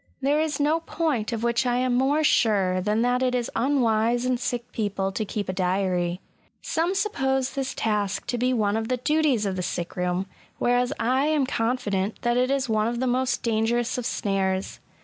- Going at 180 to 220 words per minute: Yes, average, 200 wpm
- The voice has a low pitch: No, high, 240 Hz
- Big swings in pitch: No, average, 3.9 semitones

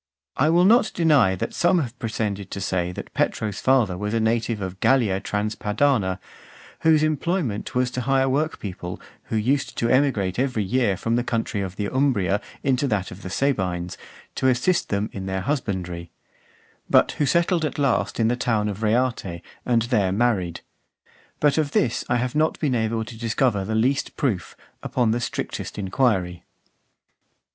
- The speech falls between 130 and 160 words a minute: No, average, 170 wpm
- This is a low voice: Yes, low, 115 Hz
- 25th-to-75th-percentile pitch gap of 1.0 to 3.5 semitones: No, average, 5.2 semitones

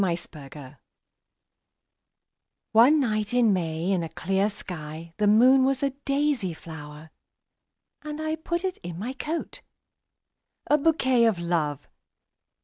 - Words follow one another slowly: Yes, slow, 110 wpm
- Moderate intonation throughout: No, wide, 8.5 semitones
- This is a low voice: No, high, 210 Hz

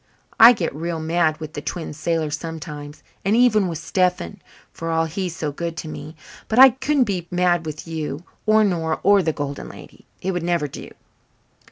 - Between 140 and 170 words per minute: No, average, 190 wpm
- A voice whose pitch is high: No, medium, 165 Hz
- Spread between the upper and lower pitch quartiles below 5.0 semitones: Yes, average, 3.0 semitones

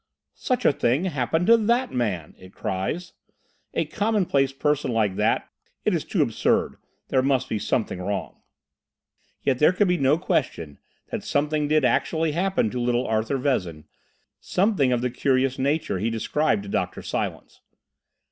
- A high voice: No, low, 135 Hz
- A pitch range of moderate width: No, wide, 6.0 semitones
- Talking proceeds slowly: No, average, 155 wpm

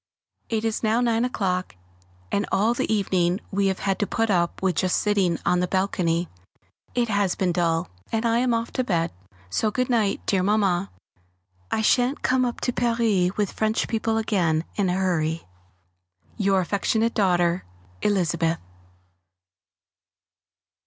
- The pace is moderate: Yes, average, 150 wpm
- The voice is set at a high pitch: Yes, high, 200 Hz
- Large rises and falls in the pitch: No, average, 3.8 semitones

